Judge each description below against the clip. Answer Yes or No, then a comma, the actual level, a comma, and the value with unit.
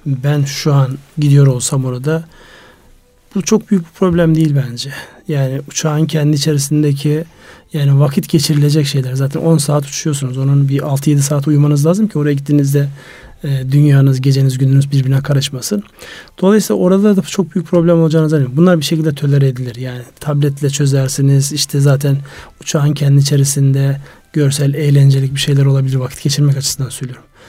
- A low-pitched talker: No, medium, 145 Hz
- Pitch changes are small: Yes, narrow, 2.2 semitones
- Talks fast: Yes, fast, 155 wpm